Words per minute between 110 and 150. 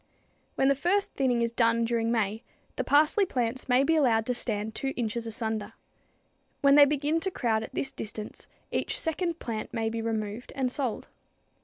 No: average, 180 wpm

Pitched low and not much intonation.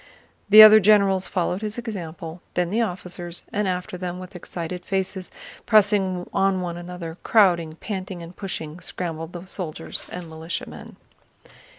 No: medium, 180 Hz; narrow, 2.1 semitones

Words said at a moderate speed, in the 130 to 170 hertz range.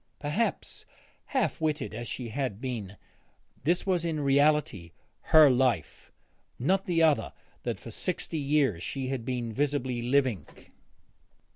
No: slow, 130 wpm; low, 135 Hz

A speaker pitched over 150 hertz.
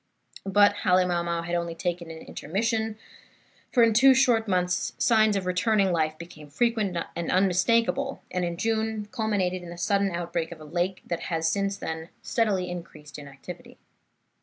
Yes: medium, 185 Hz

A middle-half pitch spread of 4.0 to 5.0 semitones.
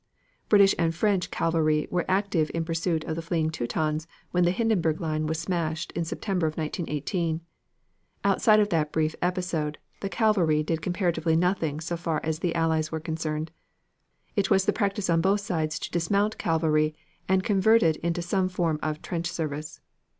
No: average, 2.9 semitones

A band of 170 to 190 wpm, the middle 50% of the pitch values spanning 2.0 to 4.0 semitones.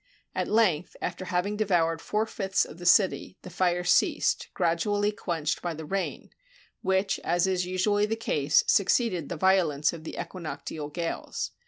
No: average, 160 wpm; average, 3.1 semitones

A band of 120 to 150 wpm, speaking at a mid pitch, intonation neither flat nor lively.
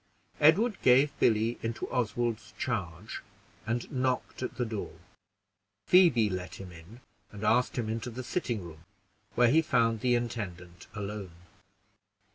No: slow, 135 wpm; low, 115 Hz; average, 3.9 semitones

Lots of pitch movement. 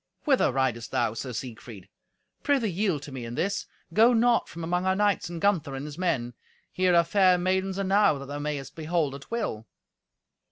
Yes: wide, 6.3 semitones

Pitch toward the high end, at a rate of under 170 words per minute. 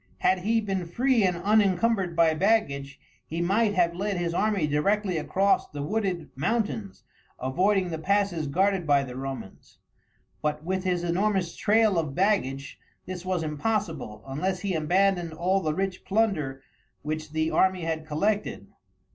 No: medium, 180 Hz; average, 150 wpm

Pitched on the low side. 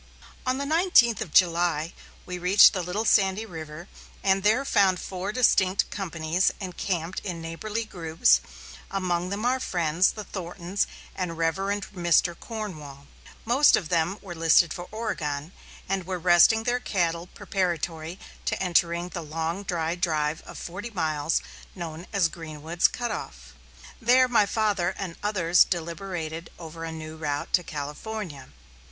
No: medium, 175 Hz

